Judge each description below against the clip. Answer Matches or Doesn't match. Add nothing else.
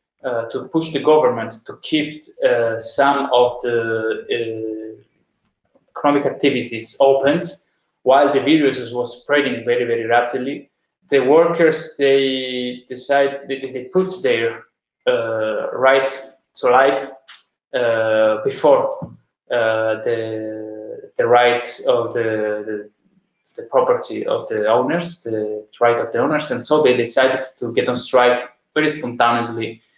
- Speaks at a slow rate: Matches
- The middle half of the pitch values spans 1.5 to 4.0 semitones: Doesn't match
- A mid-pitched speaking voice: Doesn't match